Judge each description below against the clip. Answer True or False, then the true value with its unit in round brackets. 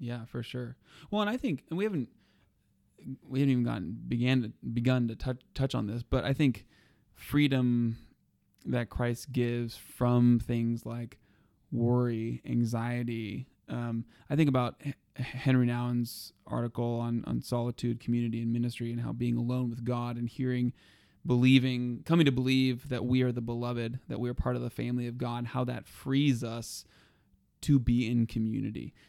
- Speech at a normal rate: True (170 wpm)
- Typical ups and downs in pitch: False (1.6 semitones)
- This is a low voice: True (120 Hz)